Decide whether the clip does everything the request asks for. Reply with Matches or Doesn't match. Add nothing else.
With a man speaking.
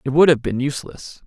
Matches